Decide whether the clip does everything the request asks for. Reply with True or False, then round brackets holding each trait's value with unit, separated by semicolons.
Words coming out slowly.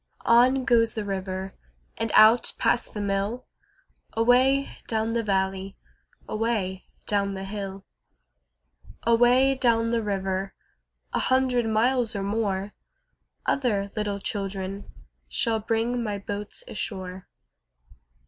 True (110 wpm)